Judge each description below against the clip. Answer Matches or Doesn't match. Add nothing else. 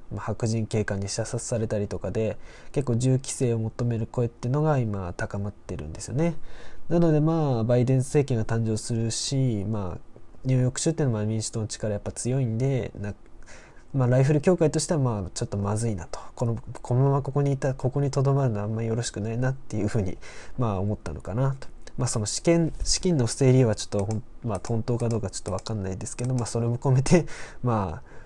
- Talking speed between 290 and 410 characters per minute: Doesn't match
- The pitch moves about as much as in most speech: Matches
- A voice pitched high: Doesn't match